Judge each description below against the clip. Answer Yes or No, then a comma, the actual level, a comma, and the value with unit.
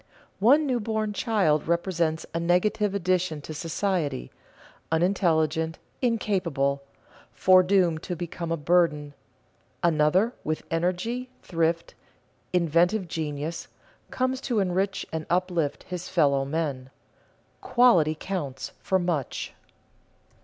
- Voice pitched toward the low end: No, medium, 175 Hz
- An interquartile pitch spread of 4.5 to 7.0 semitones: No, average, 3.7 semitones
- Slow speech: Yes, slow, 105 wpm